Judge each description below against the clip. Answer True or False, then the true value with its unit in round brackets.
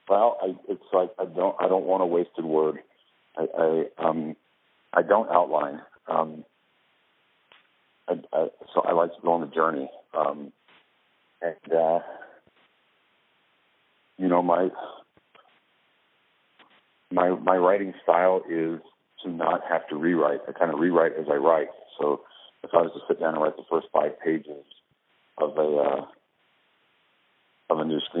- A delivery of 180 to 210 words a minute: False (155 wpm)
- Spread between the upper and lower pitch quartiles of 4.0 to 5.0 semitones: False (2.8 semitones)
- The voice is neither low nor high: False (85 Hz)